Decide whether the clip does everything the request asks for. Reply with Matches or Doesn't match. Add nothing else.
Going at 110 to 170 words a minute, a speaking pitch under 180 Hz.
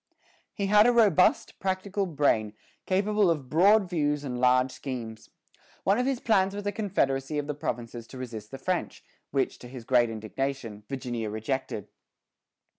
Matches